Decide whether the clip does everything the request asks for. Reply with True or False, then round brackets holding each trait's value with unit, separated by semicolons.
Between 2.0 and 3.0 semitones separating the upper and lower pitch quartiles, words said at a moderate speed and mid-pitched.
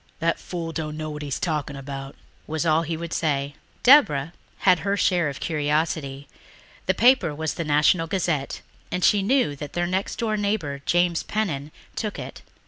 False (3.7 semitones; 170 wpm; 160 Hz)